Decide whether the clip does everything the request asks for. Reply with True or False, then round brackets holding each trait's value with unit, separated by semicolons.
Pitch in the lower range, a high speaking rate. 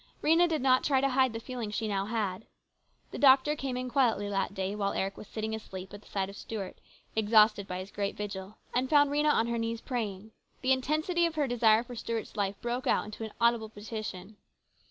False (225 Hz; 215 wpm)